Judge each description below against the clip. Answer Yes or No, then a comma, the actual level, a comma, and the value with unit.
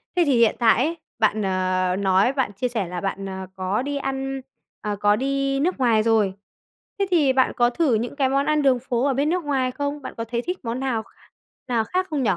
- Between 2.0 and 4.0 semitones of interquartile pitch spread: No, average, 4.6 semitones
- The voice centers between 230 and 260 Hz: Yes, very high, 250 Hz